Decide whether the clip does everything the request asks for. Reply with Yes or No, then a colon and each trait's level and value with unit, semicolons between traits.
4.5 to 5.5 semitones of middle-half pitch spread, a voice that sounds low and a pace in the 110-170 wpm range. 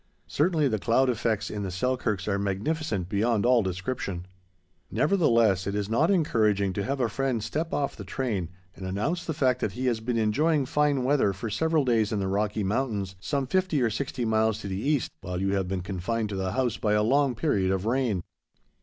No: average, 5.1 semitones; low, 110 Hz; fast, 205 wpm